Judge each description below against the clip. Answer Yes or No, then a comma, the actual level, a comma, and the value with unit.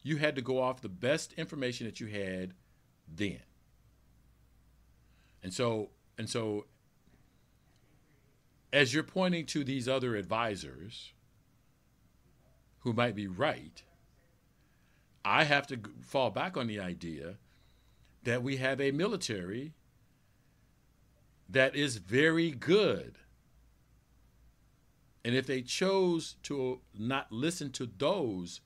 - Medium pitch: No, low, 130 Hz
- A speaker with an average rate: No, slow, 115 wpm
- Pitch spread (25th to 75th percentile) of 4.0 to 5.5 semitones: Yes, average, 4.3 semitones